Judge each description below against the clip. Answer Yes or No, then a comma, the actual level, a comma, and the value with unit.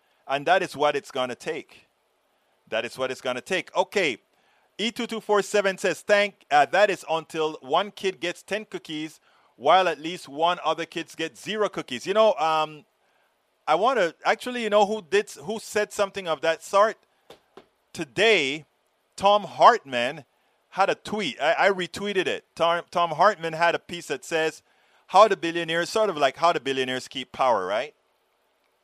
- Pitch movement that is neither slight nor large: Yes, average, 4.7 semitones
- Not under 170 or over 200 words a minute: Yes, average, 180 wpm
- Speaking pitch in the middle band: Yes, medium, 170 Hz